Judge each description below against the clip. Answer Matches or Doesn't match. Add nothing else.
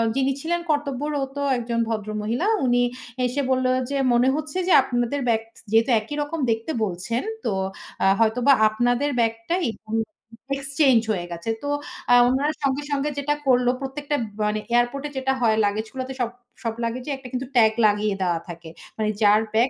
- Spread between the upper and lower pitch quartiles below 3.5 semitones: Doesn't match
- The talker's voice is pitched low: Doesn't match